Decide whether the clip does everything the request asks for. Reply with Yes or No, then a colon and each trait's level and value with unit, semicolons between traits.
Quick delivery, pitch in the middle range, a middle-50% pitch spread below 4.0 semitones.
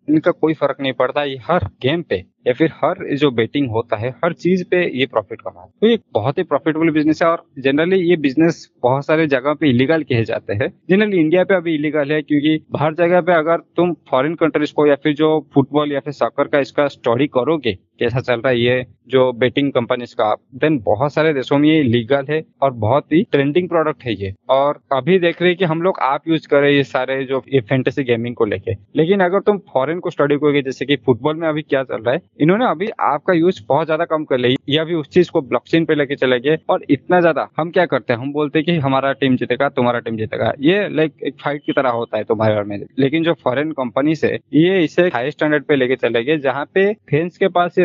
Yes: fast, 240 wpm; medium, 145 Hz; average, 3.5 semitones